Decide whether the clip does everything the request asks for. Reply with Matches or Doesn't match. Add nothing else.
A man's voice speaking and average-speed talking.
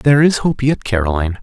Doesn't match